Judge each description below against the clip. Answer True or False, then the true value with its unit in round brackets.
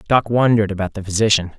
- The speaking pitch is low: True (105 Hz)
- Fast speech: False (190 wpm)